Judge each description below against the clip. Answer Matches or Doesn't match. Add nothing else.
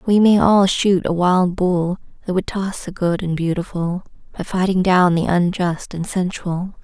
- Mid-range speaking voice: Matches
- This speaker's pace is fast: Doesn't match